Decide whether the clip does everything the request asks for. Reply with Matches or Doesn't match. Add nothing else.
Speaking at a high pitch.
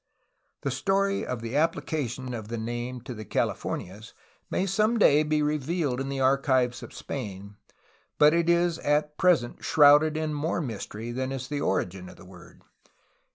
Doesn't match